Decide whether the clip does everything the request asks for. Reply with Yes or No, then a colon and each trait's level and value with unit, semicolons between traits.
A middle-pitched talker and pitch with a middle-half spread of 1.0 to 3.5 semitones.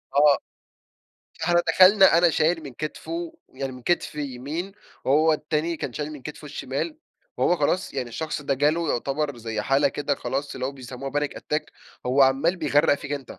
Yes: medium, 145 Hz; average, 3.1 semitones